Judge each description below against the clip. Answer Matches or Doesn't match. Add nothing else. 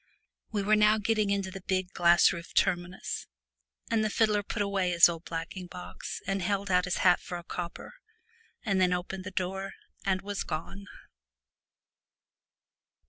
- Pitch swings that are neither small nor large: Doesn't match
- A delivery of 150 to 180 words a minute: Matches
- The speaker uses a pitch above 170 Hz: Matches